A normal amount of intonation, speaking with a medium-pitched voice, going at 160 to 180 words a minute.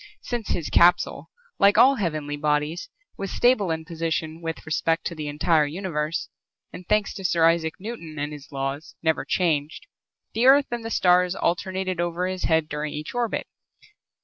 Yes: average, 3.5 semitones; medium, 165 Hz; average, 170 wpm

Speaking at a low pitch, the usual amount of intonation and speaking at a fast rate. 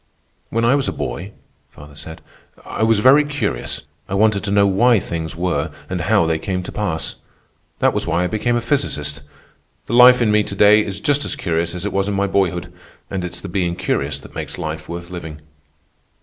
Yes: very low, 95 Hz; average, 4.2 semitones; fast, 210 wpm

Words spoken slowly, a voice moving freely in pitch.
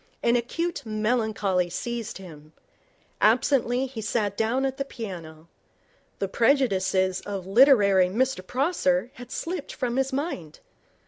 Yes: slow, 125 wpm; wide, 5.7 semitones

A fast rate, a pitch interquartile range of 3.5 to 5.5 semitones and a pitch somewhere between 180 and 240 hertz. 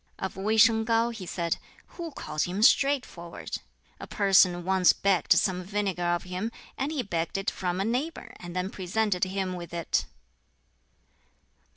No: average, 160 wpm; average, 3.8 semitones; high, 190 Hz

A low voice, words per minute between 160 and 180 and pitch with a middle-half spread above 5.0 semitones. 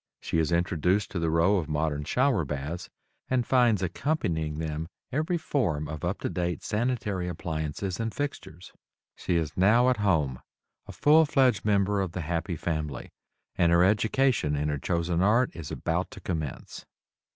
Yes: very low, 90 Hz; average, 165 wpm; wide, 5.6 semitones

